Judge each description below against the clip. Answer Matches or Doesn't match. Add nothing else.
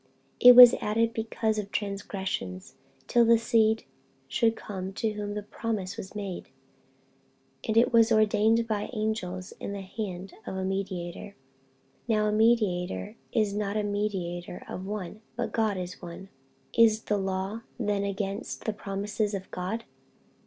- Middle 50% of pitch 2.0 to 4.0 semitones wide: Matches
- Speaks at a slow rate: Doesn't match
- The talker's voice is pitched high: Matches